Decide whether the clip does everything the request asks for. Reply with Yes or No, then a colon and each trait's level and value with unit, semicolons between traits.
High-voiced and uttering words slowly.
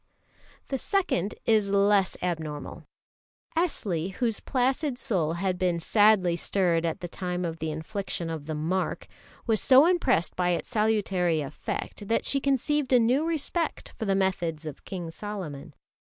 No: high, 195 Hz; average, 155 wpm